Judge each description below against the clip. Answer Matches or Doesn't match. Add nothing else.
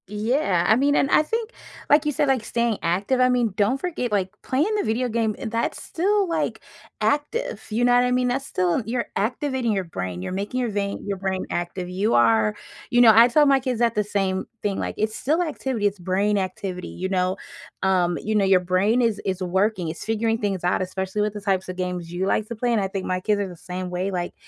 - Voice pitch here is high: Matches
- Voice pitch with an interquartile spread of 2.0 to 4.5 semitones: Doesn't match